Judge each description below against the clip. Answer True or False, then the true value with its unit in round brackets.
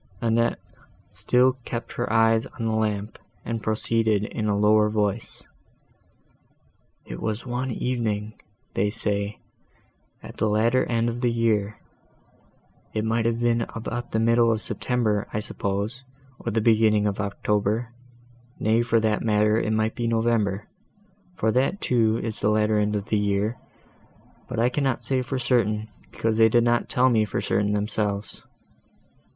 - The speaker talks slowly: False (155 wpm)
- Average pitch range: False (1.8 semitones)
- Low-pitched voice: True (110 Hz)